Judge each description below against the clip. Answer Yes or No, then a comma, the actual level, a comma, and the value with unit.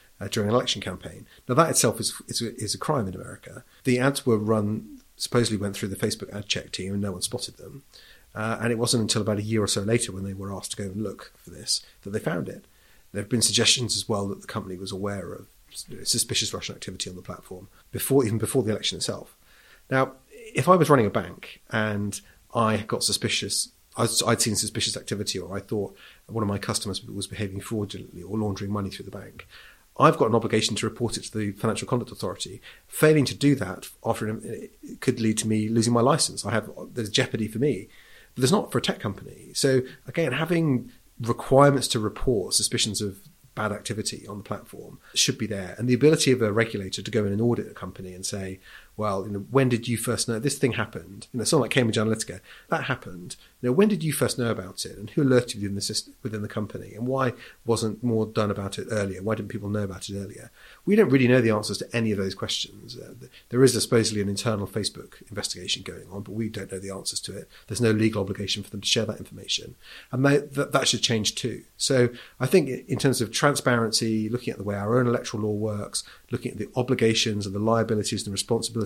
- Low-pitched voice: Yes, low, 110 Hz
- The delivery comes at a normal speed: No, fast, 235 wpm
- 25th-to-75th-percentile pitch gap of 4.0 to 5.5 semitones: No, average, 3.4 semitones